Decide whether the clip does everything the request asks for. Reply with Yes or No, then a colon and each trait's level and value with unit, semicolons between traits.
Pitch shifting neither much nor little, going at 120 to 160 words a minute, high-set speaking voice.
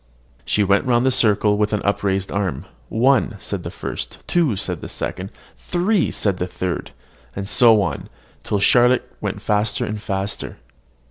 No: average, 3.6 semitones; average, 145 wpm; low, 105 Hz